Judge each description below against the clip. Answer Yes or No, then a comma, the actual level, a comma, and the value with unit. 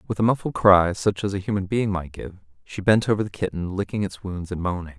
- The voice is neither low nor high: No, very low, 95 Hz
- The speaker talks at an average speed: No, fast, 255 wpm